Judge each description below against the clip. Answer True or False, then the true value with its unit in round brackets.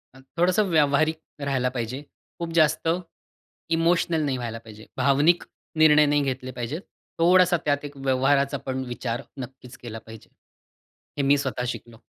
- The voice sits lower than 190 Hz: True (140 Hz)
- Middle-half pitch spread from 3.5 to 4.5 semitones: True (3.9 semitones)